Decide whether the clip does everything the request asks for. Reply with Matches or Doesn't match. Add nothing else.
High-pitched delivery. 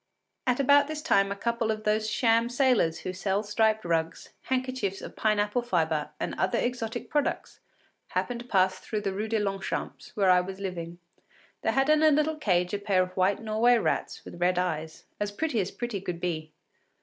Matches